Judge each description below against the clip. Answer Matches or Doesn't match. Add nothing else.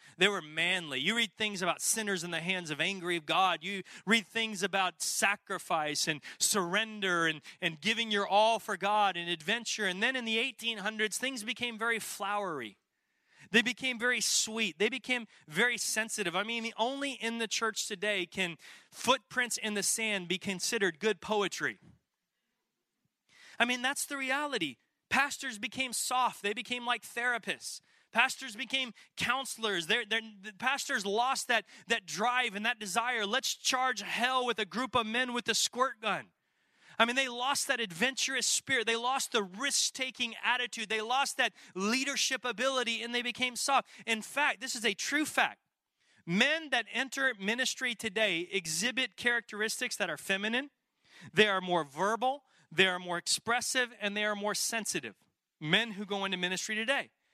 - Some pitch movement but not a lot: Matches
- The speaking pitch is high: Matches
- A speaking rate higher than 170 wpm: Doesn't match